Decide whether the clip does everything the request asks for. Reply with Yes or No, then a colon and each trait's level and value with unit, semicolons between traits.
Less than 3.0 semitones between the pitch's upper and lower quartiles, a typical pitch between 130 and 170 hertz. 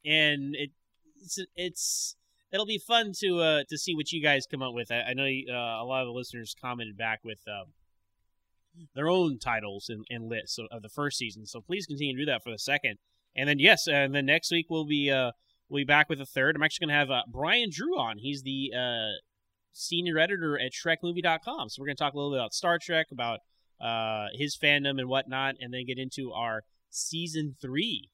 No: average, 5.3 semitones; medium, 140 Hz